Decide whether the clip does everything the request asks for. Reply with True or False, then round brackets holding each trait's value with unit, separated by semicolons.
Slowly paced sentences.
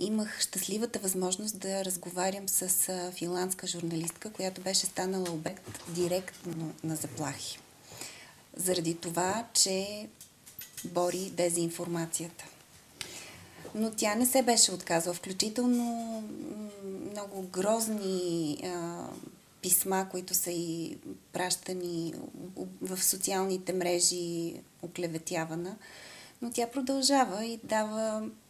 True (95 wpm)